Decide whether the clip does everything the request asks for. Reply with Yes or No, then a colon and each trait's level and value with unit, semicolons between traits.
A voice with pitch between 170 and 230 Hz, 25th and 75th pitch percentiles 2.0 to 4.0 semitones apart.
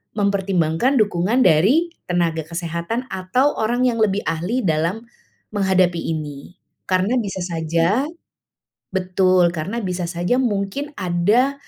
No: medium, 185 Hz; average, 4.8 semitones